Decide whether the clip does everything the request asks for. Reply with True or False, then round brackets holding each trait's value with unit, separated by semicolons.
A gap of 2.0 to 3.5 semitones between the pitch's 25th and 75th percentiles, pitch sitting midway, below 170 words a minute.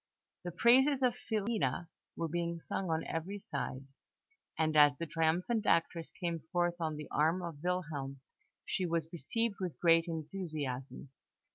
True (2.8 semitones; 170 Hz; 145 wpm)